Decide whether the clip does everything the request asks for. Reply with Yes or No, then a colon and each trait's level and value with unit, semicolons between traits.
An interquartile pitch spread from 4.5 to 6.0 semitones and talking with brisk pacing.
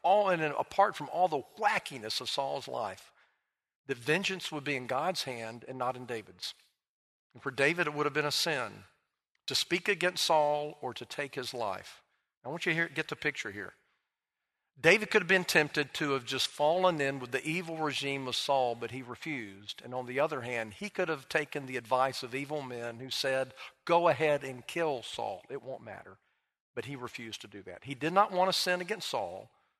Yes: average, 4.8 semitones; fast, 210 wpm